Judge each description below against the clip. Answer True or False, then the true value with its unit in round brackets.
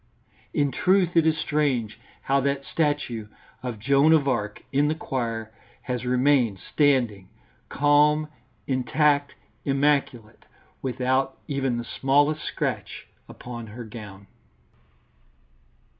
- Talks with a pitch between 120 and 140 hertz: True (135 Hz)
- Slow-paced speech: True (110 wpm)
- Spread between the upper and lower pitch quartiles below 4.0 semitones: True (3.6 semitones)